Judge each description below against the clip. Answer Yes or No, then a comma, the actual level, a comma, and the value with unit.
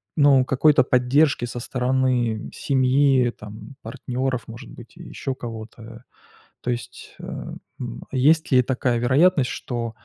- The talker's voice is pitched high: No, low, 125 Hz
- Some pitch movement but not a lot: No, narrow, 2.1 semitones